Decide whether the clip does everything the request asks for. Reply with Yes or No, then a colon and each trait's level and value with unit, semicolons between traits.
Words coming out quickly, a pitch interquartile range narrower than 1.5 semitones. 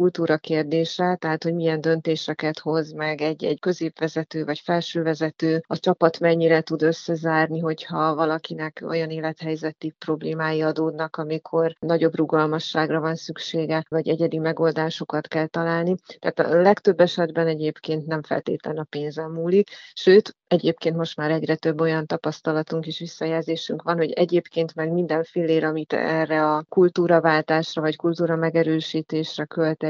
No: average, 135 wpm; narrow, 0.9 semitones